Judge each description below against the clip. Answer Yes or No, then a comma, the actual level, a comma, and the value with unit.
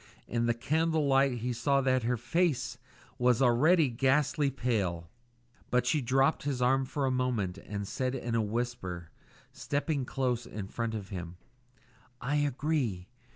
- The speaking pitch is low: Yes, low, 125 Hz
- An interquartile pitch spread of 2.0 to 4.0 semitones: Yes, average, 3.2 semitones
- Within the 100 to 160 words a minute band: Yes, average, 155 wpm